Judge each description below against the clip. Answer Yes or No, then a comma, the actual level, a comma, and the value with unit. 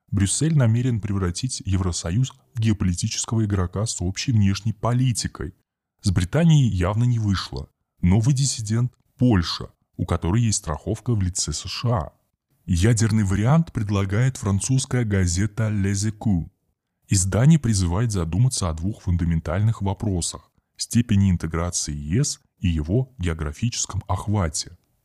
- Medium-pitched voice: No, low, 105 Hz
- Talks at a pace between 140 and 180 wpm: No, average, 115 wpm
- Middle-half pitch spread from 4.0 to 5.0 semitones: Yes, average, 4.7 semitones